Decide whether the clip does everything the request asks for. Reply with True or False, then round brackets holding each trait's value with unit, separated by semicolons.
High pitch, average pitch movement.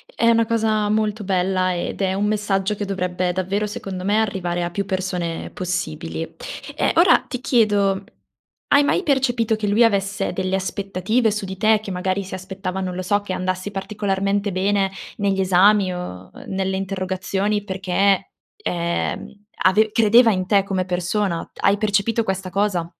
False (195 Hz; 2.1 semitones)